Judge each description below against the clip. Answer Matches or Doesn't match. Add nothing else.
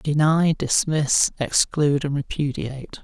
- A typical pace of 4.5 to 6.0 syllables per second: Doesn't match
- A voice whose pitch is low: Doesn't match